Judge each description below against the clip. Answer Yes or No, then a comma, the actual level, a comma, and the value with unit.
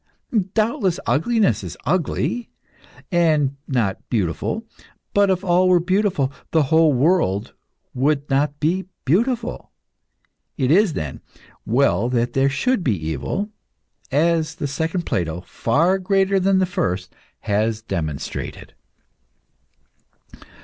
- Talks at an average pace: No, slow, 110 wpm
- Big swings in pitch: Yes, wide, 7.6 semitones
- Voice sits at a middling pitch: Yes, medium, 155 Hz